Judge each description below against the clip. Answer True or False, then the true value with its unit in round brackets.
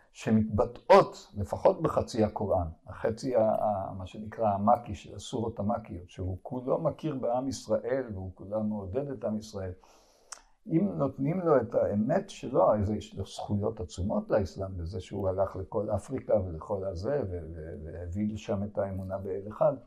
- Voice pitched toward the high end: False (100 Hz)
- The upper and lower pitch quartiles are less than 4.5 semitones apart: True (2.7 semitones)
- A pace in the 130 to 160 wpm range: True (145 wpm)